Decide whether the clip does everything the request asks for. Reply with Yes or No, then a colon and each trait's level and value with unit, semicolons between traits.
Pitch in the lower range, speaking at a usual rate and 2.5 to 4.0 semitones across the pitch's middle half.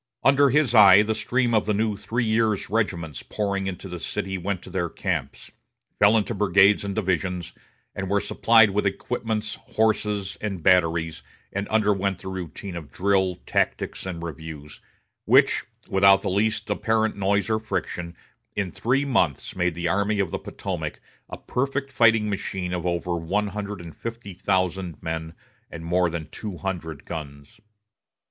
Yes: low, 100 Hz; average, 160 wpm; average, 3.5 semitones